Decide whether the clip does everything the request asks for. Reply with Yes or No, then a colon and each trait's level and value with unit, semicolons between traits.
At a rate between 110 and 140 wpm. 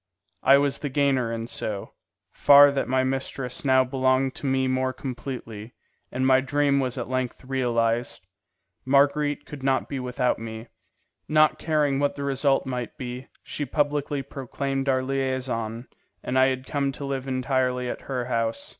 No: average, 165 wpm